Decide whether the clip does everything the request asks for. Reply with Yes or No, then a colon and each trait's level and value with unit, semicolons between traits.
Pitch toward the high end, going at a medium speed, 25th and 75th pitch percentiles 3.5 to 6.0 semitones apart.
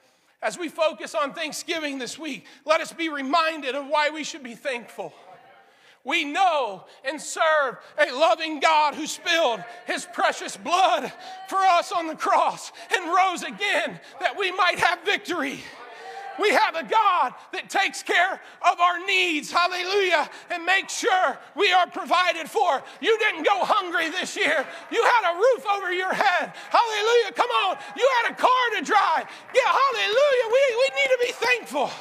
Yes: very high, 355 Hz; average, 170 wpm; average, 4.1 semitones